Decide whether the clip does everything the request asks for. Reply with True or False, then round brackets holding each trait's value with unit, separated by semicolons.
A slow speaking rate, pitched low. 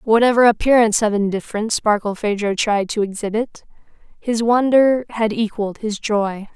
False (130 wpm; 220 Hz)